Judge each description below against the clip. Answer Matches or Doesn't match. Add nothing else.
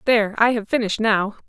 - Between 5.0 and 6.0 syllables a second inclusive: Doesn't match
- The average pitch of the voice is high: Matches